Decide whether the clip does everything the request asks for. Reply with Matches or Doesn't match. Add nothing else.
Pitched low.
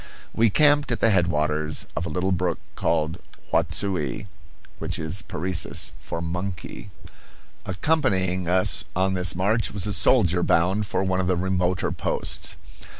Matches